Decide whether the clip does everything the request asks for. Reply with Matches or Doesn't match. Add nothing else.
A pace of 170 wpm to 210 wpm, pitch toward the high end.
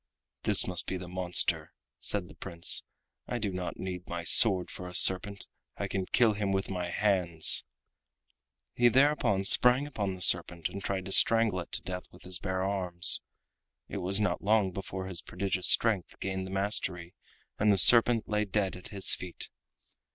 Doesn't match